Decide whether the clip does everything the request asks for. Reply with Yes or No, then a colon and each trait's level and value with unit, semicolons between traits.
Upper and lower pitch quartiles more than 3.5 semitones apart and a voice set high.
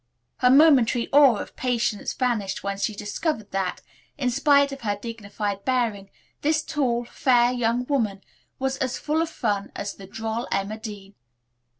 Yes: average, 4.4 semitones; high, 235 Hz